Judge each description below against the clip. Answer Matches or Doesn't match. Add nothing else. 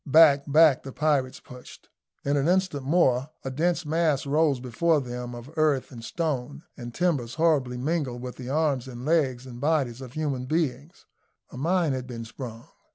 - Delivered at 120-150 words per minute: Doesn't match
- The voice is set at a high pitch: Doesn't match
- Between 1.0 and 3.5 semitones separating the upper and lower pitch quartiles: Doesn't match